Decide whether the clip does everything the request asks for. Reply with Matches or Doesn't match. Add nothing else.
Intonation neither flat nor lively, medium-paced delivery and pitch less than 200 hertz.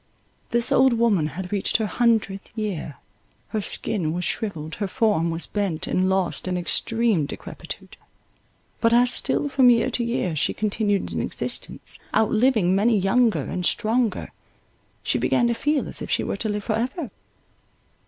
Doesn't match